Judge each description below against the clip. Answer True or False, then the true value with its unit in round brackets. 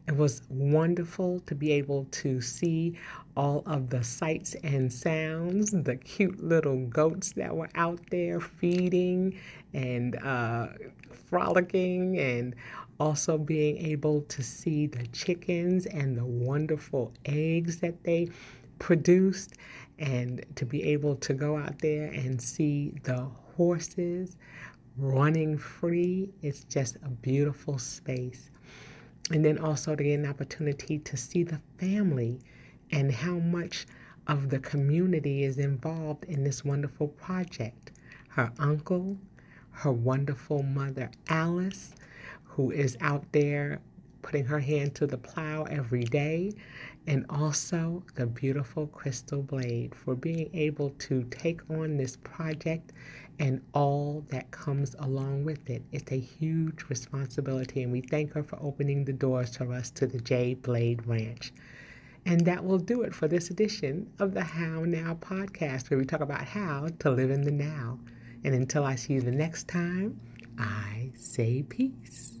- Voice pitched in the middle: True (145 Hz)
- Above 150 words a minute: False (145 wpm)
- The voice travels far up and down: False (3.8 semitones)